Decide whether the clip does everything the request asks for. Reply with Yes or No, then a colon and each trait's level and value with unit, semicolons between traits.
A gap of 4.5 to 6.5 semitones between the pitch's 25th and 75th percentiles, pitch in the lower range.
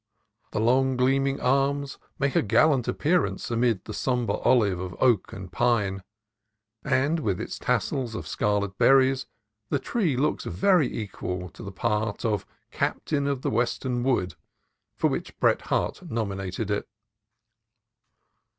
Yes: average, 4.8 semitones; low, 120 Hz